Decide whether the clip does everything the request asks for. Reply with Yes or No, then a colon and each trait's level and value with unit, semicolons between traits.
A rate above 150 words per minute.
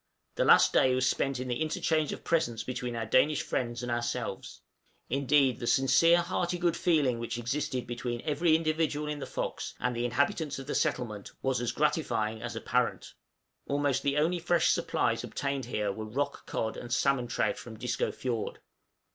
Yes: average, 180 wpm